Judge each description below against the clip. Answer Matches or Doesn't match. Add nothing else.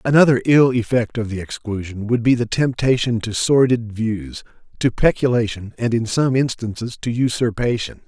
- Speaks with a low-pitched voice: Matches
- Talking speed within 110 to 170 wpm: Matches